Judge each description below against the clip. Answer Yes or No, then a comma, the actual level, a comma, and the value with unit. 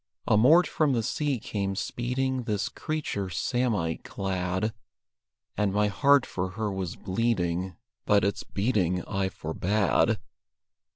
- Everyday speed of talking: No, slow, 120 wpm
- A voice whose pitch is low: Yes, low, 105 Hz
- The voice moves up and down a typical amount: Yes, average, 4.7 semitones